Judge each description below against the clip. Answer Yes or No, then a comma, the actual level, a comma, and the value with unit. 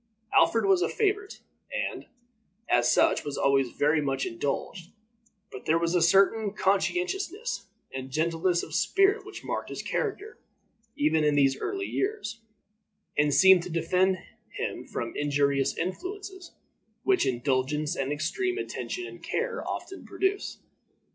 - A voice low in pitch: No, medium, 180 Hz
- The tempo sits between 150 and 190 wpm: No, average, 140 wpm